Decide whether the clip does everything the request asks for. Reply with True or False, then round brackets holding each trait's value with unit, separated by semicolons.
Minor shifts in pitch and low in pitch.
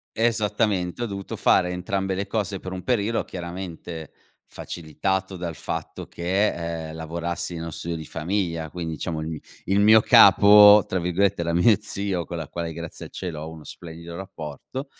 False (3.1 semitones; 90 Hz)